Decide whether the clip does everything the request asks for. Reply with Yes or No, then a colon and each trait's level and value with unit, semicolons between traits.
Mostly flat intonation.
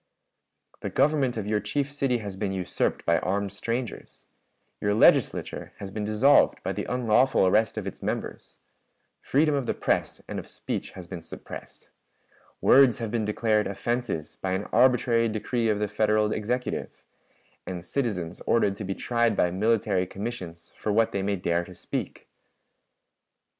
No: average, 3.6 semitones